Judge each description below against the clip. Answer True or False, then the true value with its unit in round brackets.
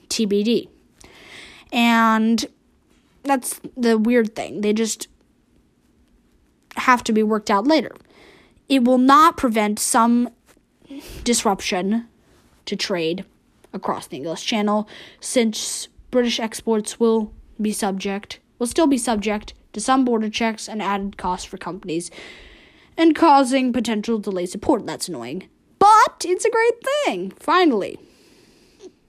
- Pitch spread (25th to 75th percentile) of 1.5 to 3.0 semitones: False (4.4 semitones)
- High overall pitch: True (230 Hz)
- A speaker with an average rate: False (120 wpm)